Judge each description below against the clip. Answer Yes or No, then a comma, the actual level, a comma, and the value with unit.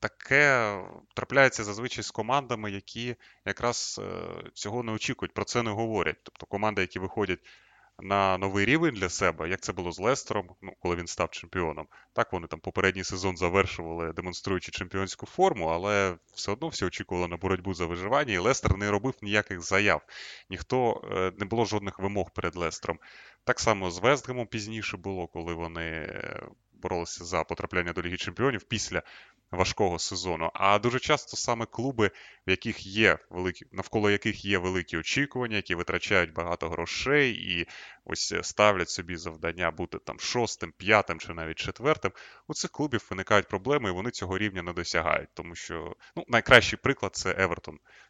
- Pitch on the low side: Yes, low, 100 Hz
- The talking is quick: Yes, fast, 165 wpm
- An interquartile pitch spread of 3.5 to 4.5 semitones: Yes, average, 3.8 semitones